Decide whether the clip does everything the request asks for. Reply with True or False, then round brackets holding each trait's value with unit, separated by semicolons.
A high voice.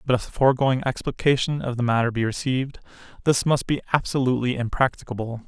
False (125 Hz)